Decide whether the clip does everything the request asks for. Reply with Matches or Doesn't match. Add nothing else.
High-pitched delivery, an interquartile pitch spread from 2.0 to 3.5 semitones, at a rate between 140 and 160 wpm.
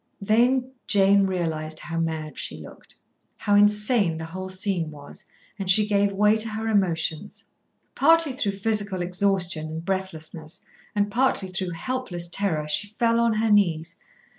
Doesn't match